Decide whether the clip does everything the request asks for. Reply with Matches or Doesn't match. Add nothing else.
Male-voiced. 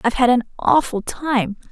Doesn't match